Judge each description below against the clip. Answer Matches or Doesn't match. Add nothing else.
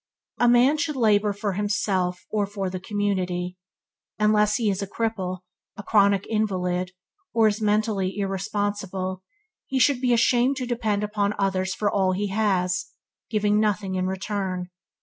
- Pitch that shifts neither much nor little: Doesn't match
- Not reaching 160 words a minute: Matches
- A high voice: Matches